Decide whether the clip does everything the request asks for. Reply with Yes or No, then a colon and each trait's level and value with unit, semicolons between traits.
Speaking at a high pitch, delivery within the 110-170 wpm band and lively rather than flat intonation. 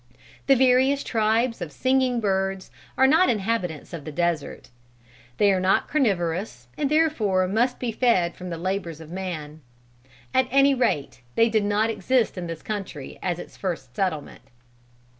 Yes: high, 200 Hz; average, 160 wpm; wide, 6.2 semitones